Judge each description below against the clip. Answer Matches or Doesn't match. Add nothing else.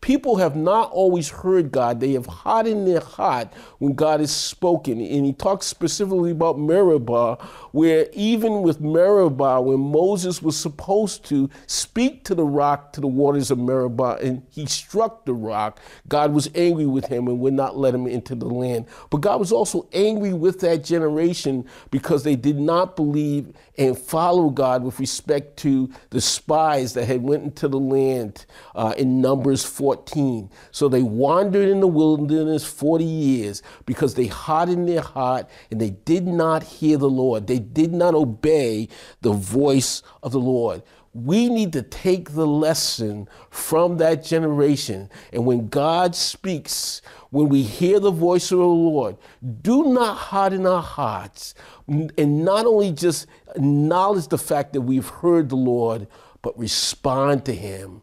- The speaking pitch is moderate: Matches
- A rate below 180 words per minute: Matches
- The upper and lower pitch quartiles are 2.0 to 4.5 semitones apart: Doesn't match